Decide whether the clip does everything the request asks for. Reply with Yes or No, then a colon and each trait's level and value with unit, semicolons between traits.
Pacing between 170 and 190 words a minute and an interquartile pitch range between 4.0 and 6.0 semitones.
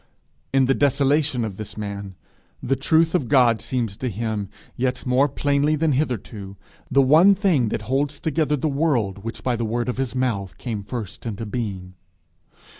Yes: average, 175 wpm; average, 4.6 semitones